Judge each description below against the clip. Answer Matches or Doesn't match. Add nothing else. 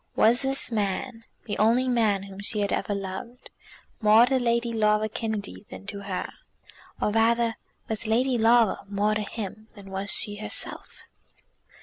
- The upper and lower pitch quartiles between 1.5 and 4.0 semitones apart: Matches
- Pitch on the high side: Matches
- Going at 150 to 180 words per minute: Matches